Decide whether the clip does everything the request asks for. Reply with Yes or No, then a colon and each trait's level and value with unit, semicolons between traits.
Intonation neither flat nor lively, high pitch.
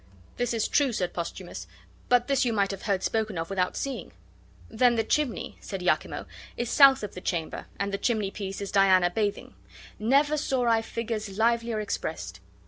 Yes: average, 3.6 semitones; high, 215 Hz